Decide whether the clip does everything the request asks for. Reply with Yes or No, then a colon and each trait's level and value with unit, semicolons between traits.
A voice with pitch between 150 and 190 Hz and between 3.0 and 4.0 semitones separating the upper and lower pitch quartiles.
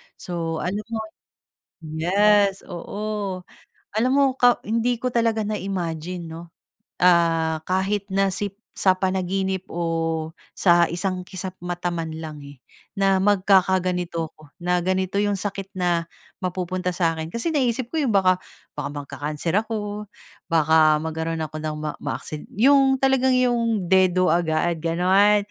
Yes: medium, 185 Hz; average, 3.7 semitones